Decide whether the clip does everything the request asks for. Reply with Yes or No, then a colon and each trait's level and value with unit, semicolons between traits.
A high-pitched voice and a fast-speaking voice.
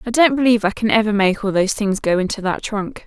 Yes: high, 210 Hz; fast, 275 wpm